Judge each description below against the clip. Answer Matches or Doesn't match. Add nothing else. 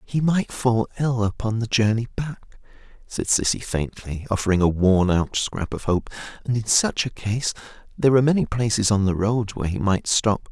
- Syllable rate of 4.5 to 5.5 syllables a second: Matches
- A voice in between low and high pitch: Doesn't match